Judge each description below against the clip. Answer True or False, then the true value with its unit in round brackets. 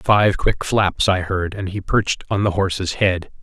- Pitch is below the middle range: True (95 Hz)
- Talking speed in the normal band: False (210 wpm)